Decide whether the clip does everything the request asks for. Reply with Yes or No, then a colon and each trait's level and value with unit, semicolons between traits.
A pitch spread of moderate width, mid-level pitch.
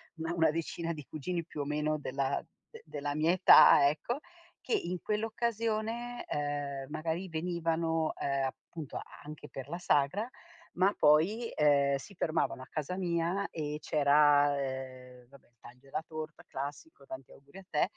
Yes: average, 3.8 semitones; medium, 155 Hz